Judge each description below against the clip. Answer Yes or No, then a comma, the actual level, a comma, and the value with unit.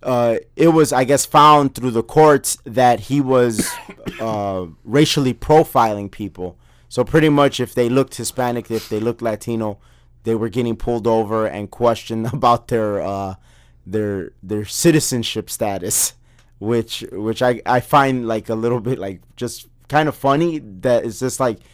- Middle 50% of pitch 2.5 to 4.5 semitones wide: Yes, average, 3.2 semitones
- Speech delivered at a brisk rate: No, average, 165 wpm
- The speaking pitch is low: Yes, low, 120 Hz